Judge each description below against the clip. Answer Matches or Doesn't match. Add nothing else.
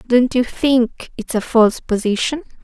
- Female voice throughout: Matches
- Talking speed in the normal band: Matches